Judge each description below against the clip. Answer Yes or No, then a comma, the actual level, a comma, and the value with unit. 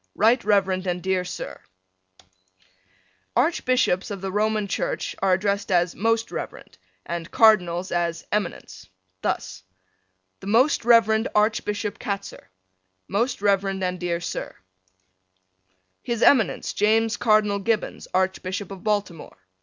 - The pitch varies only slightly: No, average, 3.1 semitones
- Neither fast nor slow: No, slow, 115 wpm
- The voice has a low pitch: No, high, 200 Hz